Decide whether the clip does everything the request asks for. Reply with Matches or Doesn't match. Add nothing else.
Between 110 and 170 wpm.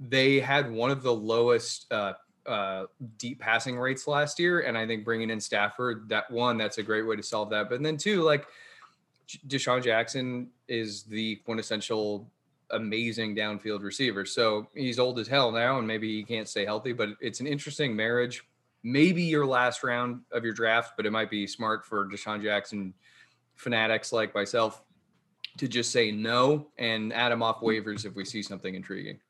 Doesn't match